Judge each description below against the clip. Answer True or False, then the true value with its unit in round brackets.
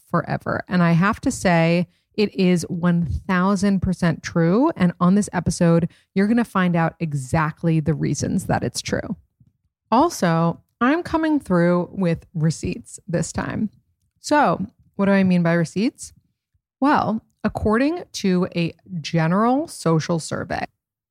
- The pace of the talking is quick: False (135 wpm)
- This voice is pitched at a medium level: True (180 Hz)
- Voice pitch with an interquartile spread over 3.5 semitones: True (4.0 semitones)